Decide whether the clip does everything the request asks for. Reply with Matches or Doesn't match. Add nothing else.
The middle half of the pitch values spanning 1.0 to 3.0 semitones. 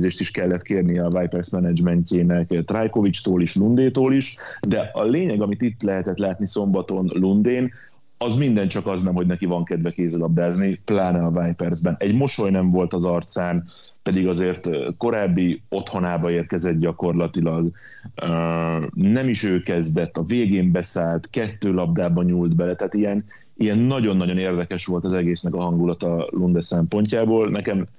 Matches